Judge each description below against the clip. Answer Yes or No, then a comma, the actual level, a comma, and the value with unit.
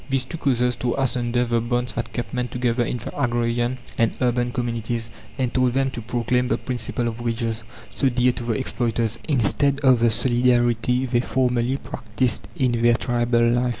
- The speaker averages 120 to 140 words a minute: No, average, 185 wpm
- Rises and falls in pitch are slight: Yes, narrow, 1.2 semitones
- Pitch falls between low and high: No, low, 120 Hz